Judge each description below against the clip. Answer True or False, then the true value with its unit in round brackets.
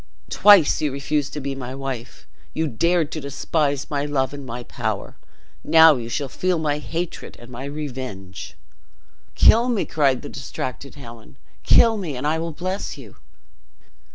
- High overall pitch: False (145 Hz)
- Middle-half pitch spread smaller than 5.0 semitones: True (3.7 semitones)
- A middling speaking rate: True (160 wpm)